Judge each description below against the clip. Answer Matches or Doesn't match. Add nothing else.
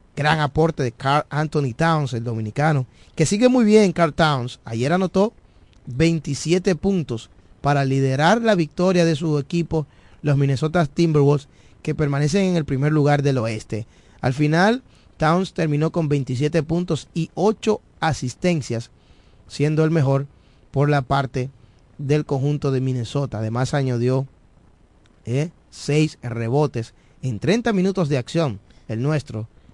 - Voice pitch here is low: Doesn't match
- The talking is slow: Doesn't match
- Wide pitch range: Doesn't match